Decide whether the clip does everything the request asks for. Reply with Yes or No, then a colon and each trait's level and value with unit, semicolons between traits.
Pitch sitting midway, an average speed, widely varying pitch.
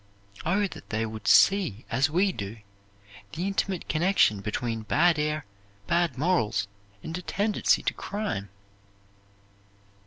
No: medium, 155 Hz; slow, 125 wpm; wide, 8.9 semitones